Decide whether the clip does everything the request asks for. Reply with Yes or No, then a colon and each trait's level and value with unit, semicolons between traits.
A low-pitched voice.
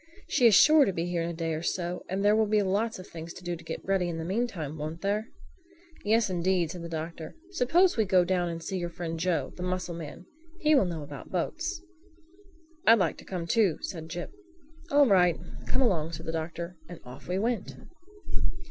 No: medium, 180 Hz